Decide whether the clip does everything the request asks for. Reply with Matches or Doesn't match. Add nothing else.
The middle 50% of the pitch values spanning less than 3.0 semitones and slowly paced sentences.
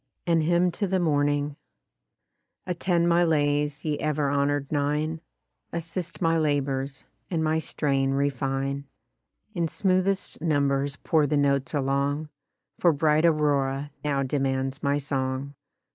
Matches